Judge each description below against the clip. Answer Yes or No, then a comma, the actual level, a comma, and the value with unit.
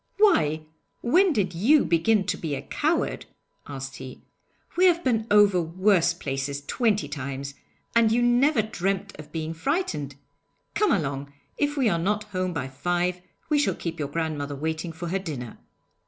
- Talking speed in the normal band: Yes, average, 165 wpm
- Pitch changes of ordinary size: No, wide, 6.8 semitones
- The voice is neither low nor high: Yes, medium, 175 Hz